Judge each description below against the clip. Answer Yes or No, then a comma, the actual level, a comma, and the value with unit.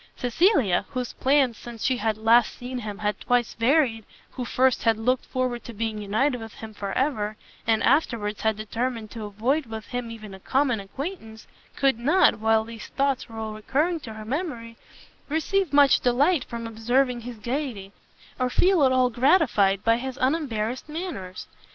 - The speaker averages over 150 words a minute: Yes, average, 175 wpm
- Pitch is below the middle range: No, high, 240 Hz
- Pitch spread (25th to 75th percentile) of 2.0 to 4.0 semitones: Yes, average, 3.6 semitones